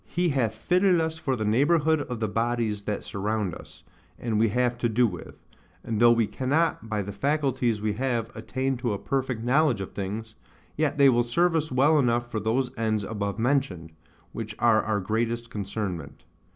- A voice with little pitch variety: No, average, 3.9 semitones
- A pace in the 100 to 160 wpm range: No, average, 190 wpm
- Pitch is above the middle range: No, low, 115 Hz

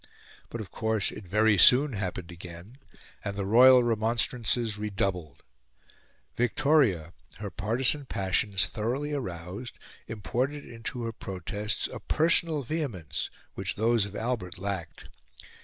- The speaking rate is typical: No, slow, 120 wpm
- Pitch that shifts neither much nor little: Yes, average, 4.4 semitones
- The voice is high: No, low, 110 Hz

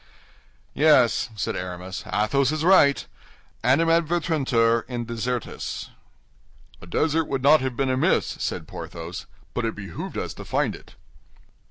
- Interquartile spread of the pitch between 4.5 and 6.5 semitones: Yes, average, 5.2 semitones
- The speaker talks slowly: Yes, slow, 130 wpm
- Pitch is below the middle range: Yes, low, 130 Hz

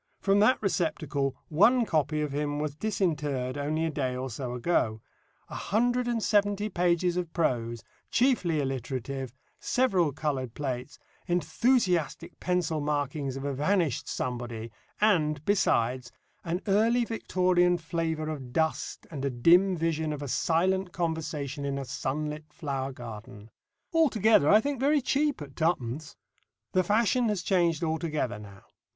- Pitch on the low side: No, medium, 160 Hz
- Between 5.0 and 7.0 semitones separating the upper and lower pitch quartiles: Yes, wide, 5.4 semitones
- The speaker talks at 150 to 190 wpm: No, average, 140 wpm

